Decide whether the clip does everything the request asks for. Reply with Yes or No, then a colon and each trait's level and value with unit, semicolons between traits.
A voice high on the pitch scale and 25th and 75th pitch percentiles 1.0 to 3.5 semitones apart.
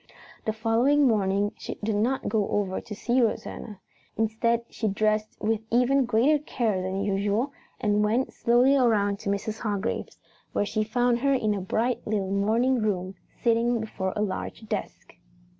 Yes: high, 220 Hz; narrow, 2.6 semitones